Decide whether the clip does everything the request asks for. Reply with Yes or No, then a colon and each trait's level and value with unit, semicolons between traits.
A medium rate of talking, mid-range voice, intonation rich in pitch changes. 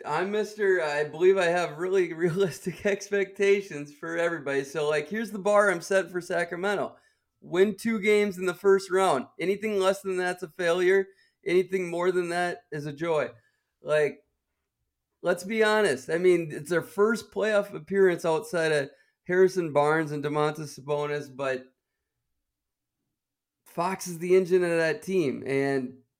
No: average, 155 wpm; medium, 180 Hz; average, 4.5 semitones